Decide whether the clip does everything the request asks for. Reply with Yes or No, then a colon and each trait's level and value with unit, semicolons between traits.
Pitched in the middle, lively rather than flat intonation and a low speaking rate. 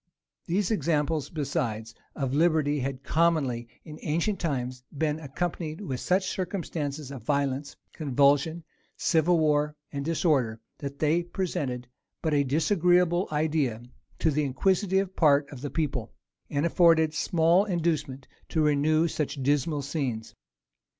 No: medium, 150 Hz; average, 3.3 semitones; slow, 130 wpm